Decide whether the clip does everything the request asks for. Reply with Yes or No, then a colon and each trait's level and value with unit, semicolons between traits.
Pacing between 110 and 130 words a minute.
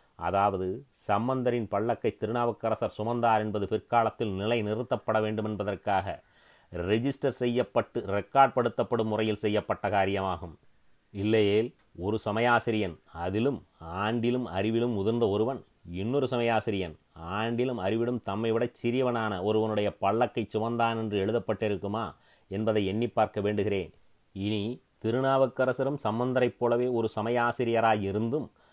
No: average, 100 wpm